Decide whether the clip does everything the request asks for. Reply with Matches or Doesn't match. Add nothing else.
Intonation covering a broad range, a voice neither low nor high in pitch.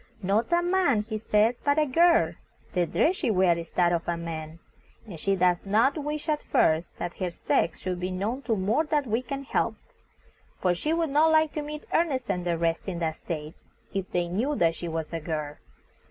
Doesn't match